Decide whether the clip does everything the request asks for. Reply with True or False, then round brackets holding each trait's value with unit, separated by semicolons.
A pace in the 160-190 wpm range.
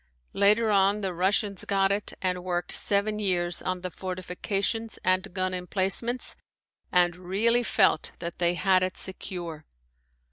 False (140 wpm)